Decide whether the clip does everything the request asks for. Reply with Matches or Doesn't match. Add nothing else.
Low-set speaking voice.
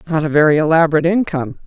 Doesn't match